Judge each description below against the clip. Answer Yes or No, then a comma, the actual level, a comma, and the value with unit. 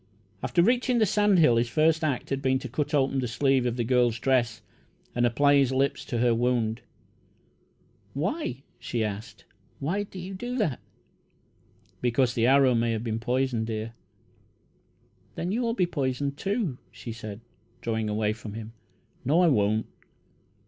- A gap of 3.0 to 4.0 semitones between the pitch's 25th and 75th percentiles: No, average, 5.1 semitones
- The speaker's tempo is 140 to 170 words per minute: Yes, average, 160 wpm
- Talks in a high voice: No, low, 130 Hz